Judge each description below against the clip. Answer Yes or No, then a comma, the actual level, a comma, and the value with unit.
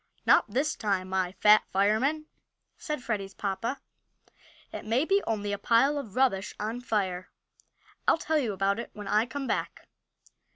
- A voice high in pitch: Yes, high, 215 Hz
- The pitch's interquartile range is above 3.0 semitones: Yes, average, 5.1 semitones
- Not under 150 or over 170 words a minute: Yes, average, 160 wpm